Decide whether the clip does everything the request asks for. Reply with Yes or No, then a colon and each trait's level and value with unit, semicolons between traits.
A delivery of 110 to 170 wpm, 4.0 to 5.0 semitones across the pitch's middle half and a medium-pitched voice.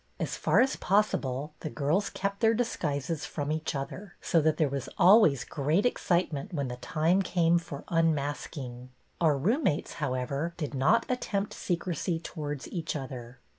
Yes: average, 165 wpm; average, 4.7 semitones; medium, 155 Hz